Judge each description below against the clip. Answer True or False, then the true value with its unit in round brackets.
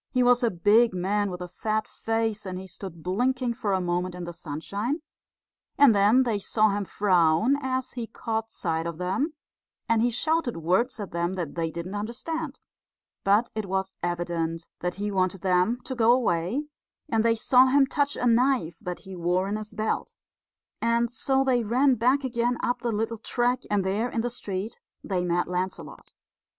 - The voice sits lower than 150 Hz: False (215 Hz)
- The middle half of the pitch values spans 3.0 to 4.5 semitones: False (5.0 semitones)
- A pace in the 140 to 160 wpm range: False (185 wpm)